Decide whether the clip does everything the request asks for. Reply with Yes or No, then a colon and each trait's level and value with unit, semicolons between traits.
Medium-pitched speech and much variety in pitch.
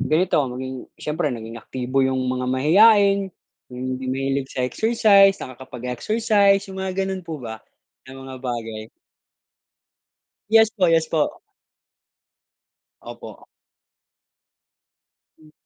Yes: medium, 150 Hz; wide, 7.3 semitones